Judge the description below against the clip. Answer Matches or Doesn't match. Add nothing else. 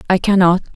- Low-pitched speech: Doesn't match